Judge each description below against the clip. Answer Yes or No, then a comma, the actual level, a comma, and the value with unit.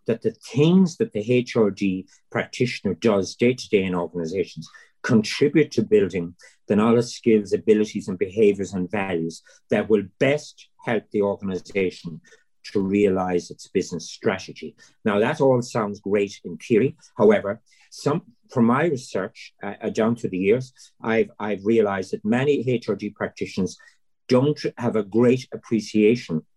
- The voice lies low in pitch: Yes, low, 110 Hz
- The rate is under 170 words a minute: Yes, average, 145 wpm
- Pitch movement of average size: Yes, average, 4.1 semitones